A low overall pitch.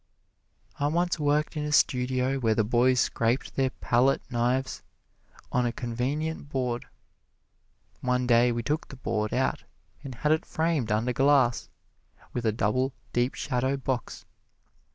Yes: low, 125 Hz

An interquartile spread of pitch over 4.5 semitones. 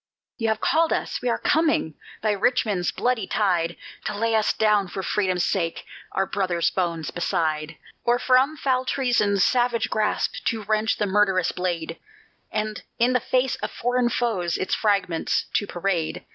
Yes: average, 4.9 semitones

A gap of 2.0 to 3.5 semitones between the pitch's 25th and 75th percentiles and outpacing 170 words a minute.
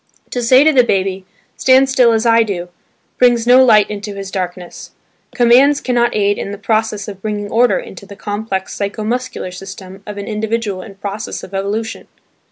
Yes: average, 3.2 semitones; average, 180 wpm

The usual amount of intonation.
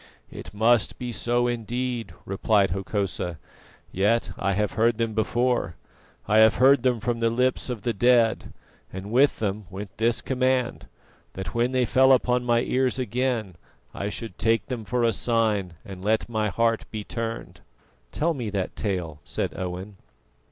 Yes: average, 3.2 semitones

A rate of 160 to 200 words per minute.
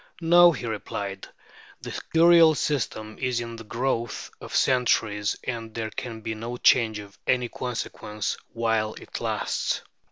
No: slow, 135 wpm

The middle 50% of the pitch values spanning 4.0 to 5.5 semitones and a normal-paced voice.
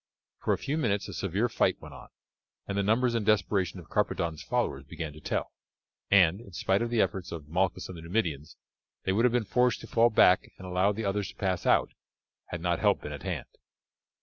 No: average, 4.6 semitones; fast, 220 wpm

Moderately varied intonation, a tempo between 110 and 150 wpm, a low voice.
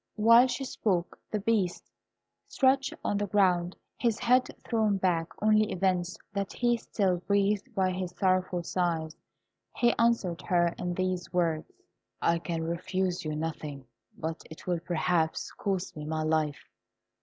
No: average, 3.7 semitones; average, 145 wpm; medium, 185 Hz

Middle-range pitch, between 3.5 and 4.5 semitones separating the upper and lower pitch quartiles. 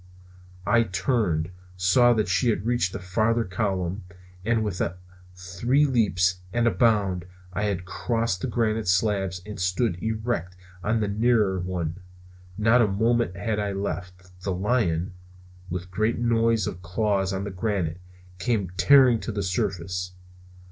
No: low, 100 Hz; average, 3.9 semitones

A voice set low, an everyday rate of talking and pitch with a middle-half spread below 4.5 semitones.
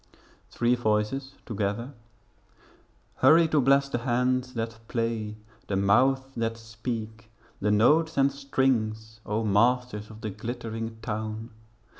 No: low, 115 Hz; slow, 120 wpm; average, 2.9 semitones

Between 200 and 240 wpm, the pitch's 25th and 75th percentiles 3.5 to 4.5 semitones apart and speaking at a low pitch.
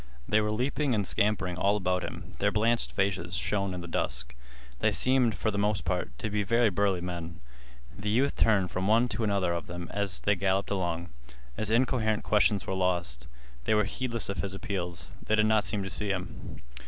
No: fast, 205 wpm; average, 3.1 semitones; low, 100 Hz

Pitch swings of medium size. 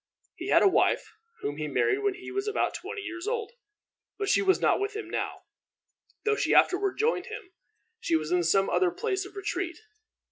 Yes: average, 3.1 semitones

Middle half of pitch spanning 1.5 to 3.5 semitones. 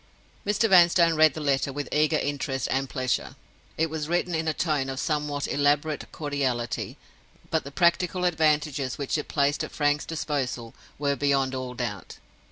Yes: average, 2.7 semitones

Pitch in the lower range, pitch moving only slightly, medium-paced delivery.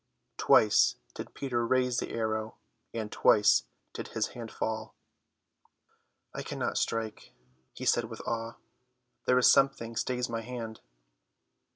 No: low, 115 Hz; narrow, 1.8 semitones; slow, 130 wpm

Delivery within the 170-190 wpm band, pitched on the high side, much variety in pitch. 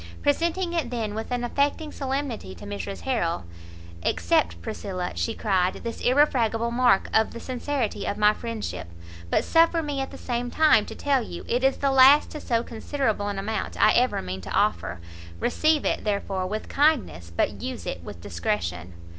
Yes: average, 180 wpm; high, 230 Hz; wide, 6.7 semitones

